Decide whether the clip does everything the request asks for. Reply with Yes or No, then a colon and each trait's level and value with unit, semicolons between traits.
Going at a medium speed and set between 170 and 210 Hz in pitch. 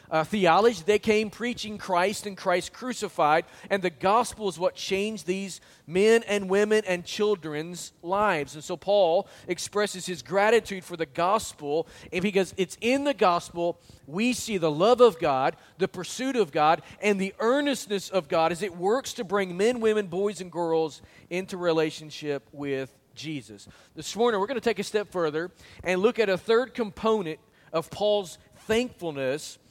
Yes: average, 170 wpm; high, 190 Hz